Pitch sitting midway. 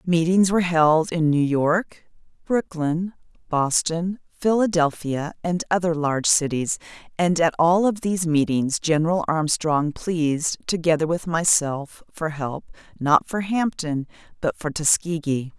Yes: medium, 165 Hz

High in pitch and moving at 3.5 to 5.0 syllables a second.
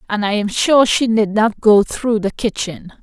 Yes: high, 215 Hz; 4.4 syllables/s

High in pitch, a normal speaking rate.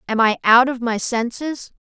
Yes: high, 240 Hz; average, 195 wpm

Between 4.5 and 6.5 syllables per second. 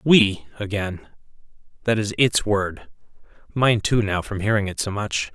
No: 4.2 syllables/s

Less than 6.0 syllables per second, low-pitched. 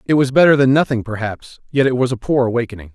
No: 6.6 syllables/s; low, 125 Hz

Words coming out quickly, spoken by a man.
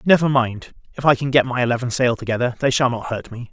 Yes: fast, 255 wpm; male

